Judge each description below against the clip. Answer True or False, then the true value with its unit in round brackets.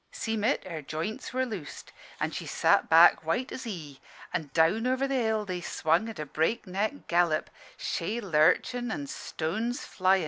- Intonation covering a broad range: True (6.2 semitones)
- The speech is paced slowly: False (170 wpm)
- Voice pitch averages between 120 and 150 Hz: False (190 Hz)